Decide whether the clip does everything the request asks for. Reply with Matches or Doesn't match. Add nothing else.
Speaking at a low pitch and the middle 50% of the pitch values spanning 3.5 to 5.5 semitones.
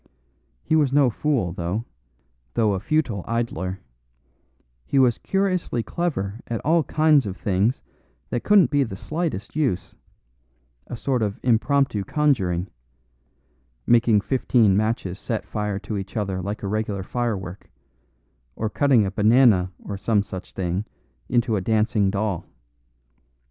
Matches